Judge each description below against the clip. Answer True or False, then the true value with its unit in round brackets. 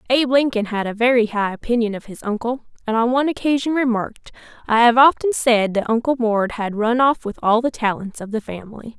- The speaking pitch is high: True (235 Hz)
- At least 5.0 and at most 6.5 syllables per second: True (5.9 syllables/s)